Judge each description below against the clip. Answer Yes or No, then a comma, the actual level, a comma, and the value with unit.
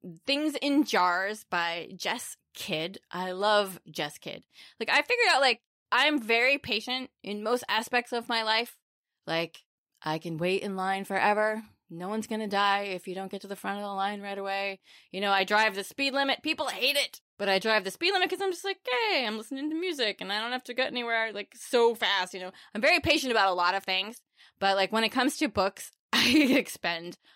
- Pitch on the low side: No, high, 215 Hz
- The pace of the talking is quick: Yes, fast, 220 wpm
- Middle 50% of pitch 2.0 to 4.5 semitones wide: No, average, 5.1 semitones